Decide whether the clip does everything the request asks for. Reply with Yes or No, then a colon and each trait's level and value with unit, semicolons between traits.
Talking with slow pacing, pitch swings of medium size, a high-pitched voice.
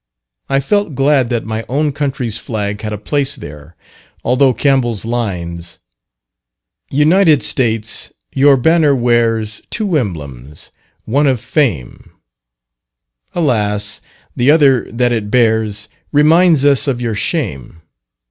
No: slow, 120 wpm; average, 5.0 semitones; low, 120 Hz